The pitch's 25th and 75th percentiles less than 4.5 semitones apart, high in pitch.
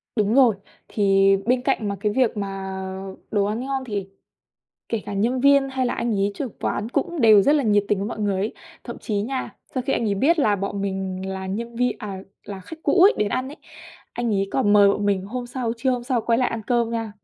Yes: average, 3.9 semitones; high, 220 Hz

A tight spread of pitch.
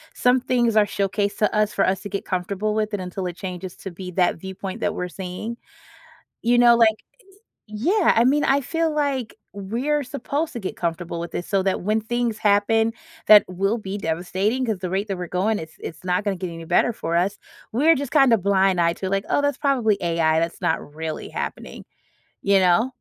No: average, 4.4 semitones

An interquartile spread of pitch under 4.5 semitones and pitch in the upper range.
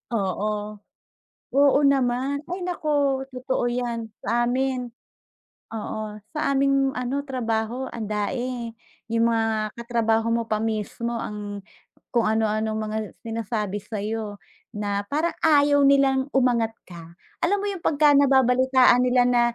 Yes: average, 3.6 semitones; high, 240 Hz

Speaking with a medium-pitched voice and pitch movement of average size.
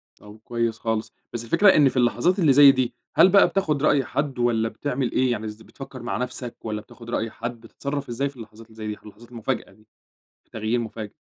No: low, 120 Hz; average, 3.6 semitones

